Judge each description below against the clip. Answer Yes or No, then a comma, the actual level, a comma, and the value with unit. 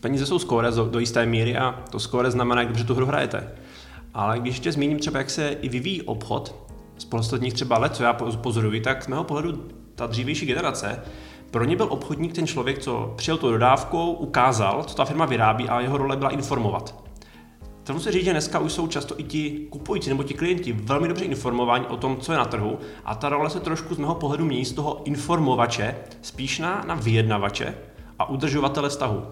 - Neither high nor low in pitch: No, low, 130 Hz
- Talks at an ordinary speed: No, fast, 205 wpm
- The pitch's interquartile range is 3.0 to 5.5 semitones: Yes, average, 4.1 semitones